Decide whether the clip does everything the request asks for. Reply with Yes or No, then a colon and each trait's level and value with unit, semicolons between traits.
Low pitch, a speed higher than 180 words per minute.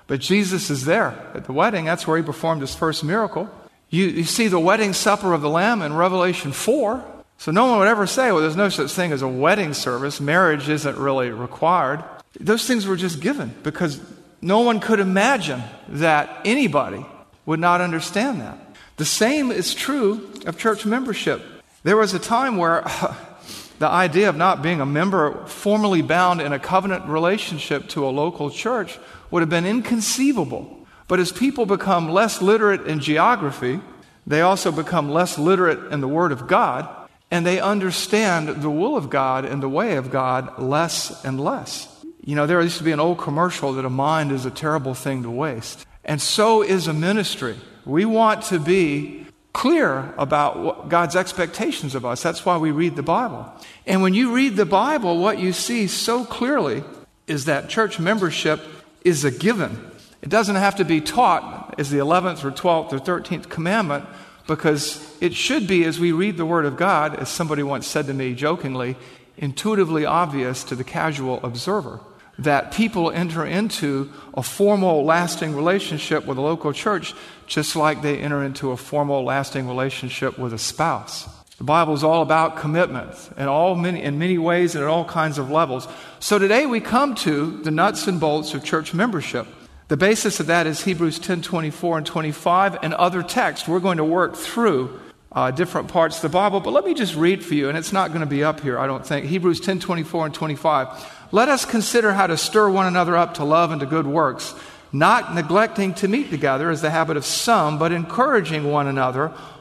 No: medium, 170 Hz; average, 195 wpm